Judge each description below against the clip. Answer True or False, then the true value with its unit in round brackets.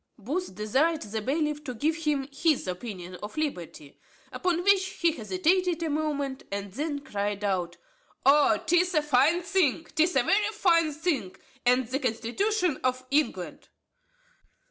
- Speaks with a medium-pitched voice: False (295 Hz)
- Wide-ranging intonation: True (6.4 semitones)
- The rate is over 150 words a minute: False (145 wpm)